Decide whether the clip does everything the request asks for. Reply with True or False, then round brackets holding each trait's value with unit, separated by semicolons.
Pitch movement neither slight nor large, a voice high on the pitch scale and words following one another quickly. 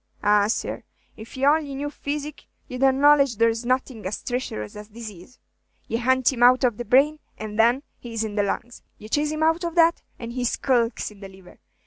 True (4.3 semitones; 245 Hz; 215 wpm)